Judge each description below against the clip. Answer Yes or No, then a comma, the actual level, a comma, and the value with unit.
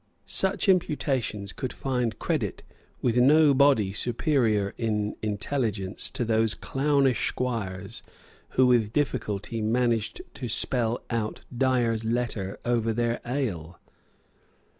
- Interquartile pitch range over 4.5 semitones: No, average, 3.3 semitones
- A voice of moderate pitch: No, low, 115 Hz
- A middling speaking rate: No, slow, 110 wpm